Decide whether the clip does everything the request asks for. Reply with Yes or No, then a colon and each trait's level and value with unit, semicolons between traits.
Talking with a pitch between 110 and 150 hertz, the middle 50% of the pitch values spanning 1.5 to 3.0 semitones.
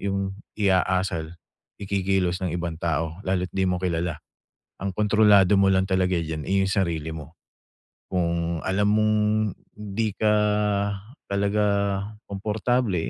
No: very low, 95 Hz; average, 2.7 semitones